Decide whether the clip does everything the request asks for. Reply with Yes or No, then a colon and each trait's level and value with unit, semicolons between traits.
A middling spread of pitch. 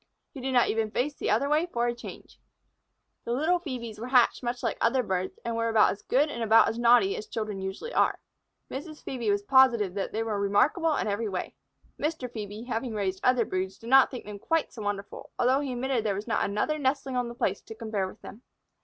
Yes: average, 4.1 semitones